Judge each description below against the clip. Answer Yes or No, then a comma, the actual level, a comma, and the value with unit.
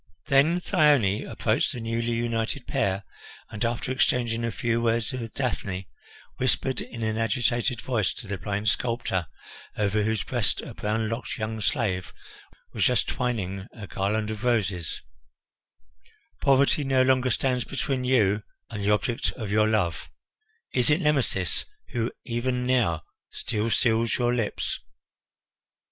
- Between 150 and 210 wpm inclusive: No, average, 140 wpm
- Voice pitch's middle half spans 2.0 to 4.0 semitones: Yes, average, 3.0 semitones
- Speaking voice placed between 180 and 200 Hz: No, low, 115 Hz